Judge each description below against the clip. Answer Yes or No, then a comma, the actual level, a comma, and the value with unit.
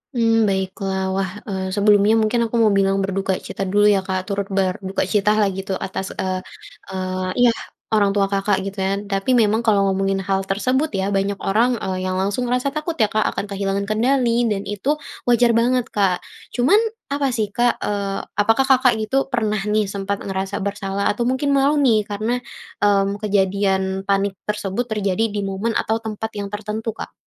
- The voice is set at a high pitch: Yes, high, 205 Hz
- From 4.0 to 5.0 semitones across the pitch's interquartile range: No, narrow, 2.6 semitones